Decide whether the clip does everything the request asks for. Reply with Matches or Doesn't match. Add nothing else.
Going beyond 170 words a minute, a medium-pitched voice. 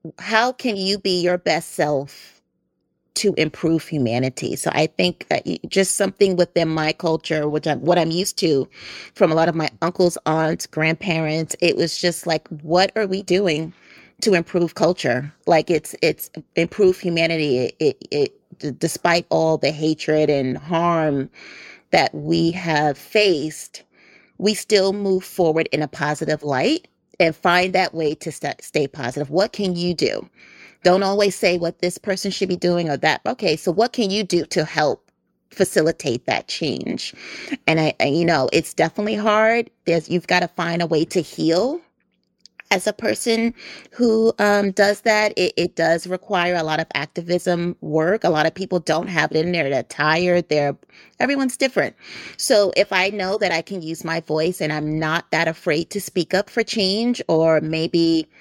Matches